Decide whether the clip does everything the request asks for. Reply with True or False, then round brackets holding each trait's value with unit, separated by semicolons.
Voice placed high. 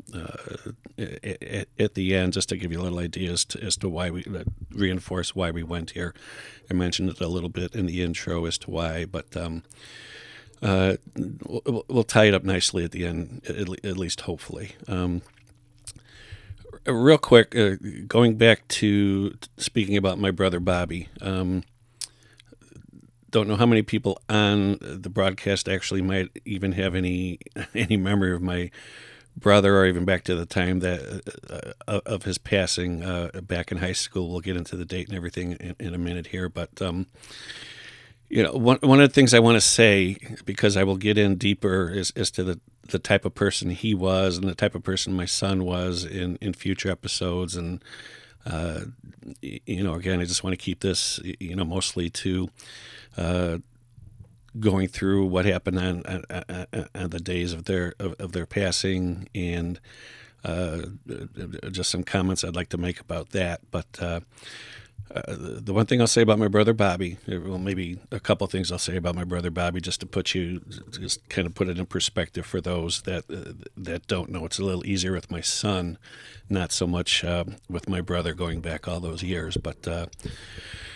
False (95 Hz)